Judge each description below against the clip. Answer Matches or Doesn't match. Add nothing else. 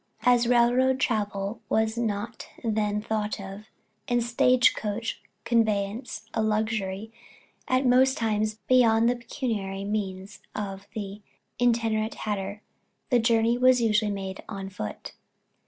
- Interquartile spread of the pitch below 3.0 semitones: Matches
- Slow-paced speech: Matches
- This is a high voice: Matches